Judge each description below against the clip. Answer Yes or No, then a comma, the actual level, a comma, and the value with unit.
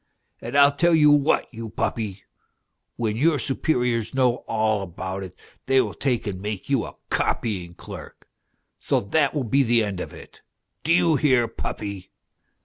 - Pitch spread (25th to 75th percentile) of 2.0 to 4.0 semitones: No, wide, 5.4 semitones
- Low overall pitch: Yes, low, 120 Hz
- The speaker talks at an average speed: Yes, average, 165 wpm